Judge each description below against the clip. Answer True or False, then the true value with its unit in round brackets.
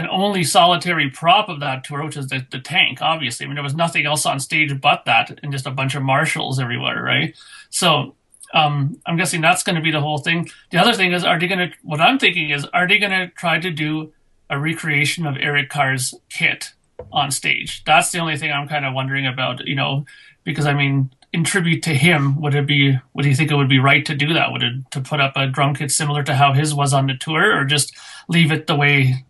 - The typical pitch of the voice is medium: True (145 Hz)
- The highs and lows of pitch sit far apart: False (2.8 semitones)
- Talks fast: True (250 wpm)